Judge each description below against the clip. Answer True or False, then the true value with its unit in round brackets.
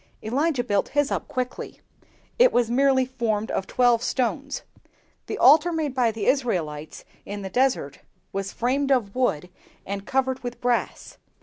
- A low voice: False (245 Hz)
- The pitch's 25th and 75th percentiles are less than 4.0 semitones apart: False (4.4 semitones)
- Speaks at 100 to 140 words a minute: False (150 wpm)